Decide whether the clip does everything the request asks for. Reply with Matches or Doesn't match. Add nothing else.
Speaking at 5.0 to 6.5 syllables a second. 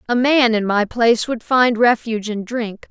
Doesn't match